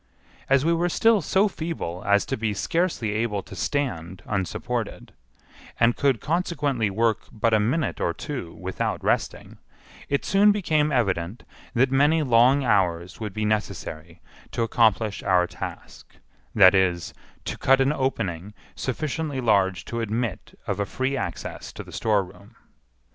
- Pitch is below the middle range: Yes, low, 115 Hz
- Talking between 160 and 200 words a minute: No, average, 145 wpm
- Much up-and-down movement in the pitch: Yes, wide, 6.4 semitones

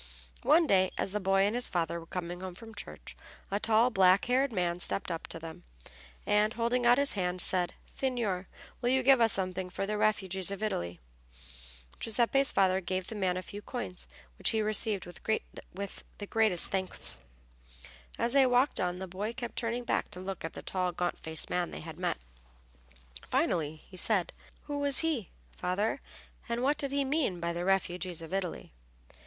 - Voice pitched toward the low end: No, high, 195 Hz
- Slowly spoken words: No, average, 185 wpm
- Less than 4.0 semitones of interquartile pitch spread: No, average, 4.5 semitones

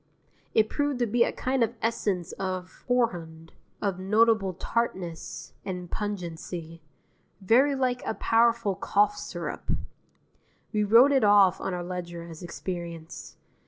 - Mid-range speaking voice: No, high, 200 Hz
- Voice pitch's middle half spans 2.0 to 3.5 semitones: No, average, 4.8 semitones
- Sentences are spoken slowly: Yes, slow, 130 wpm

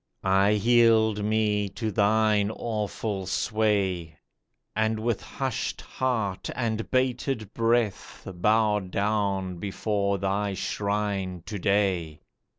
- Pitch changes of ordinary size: No, narrow, 2.1 semitones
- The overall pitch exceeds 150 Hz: No, low, 105 Hz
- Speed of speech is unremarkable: No, slow, 100 wpm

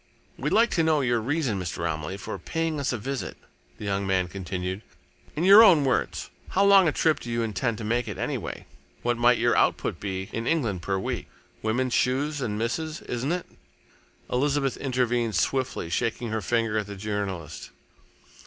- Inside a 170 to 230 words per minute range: Yes, average, 180 wpm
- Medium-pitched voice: No, low, 120 Hz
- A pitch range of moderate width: No, wide, 5.9 semitones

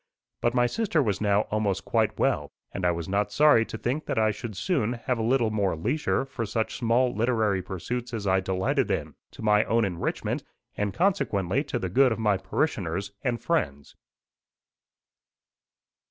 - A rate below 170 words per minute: No, average, 175 wpm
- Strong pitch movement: No, average, 4.1 semitones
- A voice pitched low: Yes, low, 110 Hz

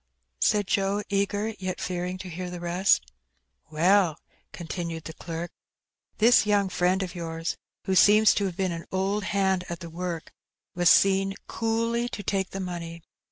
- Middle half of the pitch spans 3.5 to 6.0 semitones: No, narrow, 2.5 semitones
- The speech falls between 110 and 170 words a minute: Yes, average, 160 wpm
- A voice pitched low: No, medium, 185 Hz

